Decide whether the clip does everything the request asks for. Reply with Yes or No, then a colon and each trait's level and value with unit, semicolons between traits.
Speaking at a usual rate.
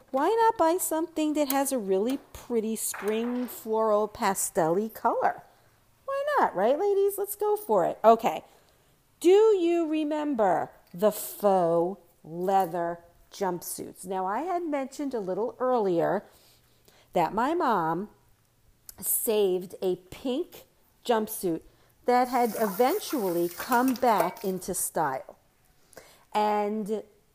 No: slow, 110 wpm